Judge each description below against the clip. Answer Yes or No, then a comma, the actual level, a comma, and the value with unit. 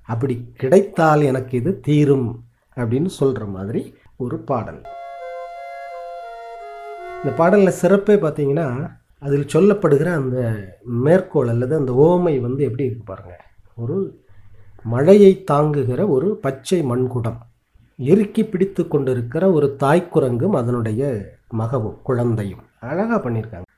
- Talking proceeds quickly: No, average, 105 wpm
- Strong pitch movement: Yes, wide, 6.5 semitones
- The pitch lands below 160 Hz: Yes, medium, 140 Hz